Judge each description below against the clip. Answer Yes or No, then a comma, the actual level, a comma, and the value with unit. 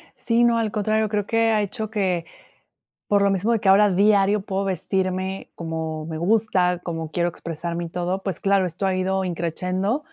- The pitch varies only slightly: No, average, 3.1 semitones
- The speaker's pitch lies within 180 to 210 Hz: Yes, high, 190 Hz